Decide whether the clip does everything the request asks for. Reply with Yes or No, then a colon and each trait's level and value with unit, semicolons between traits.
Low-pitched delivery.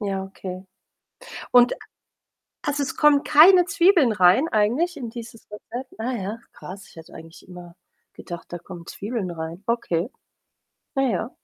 No: high, 220 Hz